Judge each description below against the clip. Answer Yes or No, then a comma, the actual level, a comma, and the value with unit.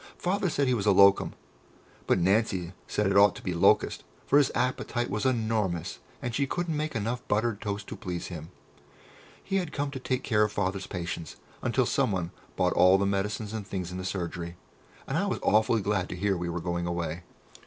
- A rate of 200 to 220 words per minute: Yes, fast, 205 wpm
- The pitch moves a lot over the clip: No, average, 4.8 semitones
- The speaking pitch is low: Yes, low, 100 Hz